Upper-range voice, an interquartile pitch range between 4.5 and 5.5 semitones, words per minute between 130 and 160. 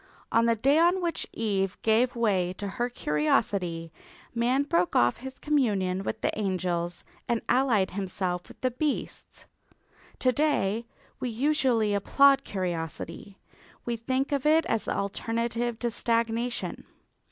Yes: high, 230 Hz; average, 5.1 semitones; average, 140 wpm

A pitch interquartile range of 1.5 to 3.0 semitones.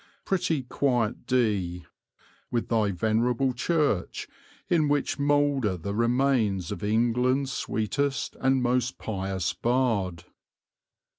No: average, 4.5 semitones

